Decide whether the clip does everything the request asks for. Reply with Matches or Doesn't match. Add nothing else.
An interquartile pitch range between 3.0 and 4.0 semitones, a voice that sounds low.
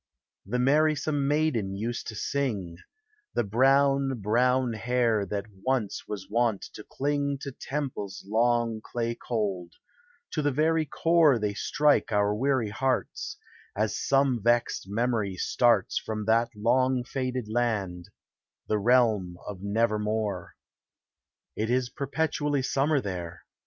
Doesn't match